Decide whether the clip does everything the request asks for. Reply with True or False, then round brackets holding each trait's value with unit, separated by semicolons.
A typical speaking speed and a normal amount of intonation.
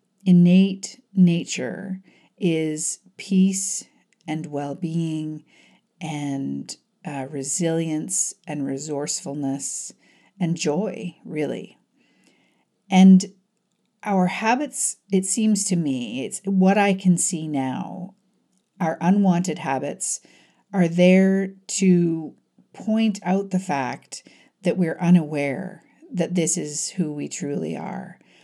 False (100 wpm; 3.9 semitones)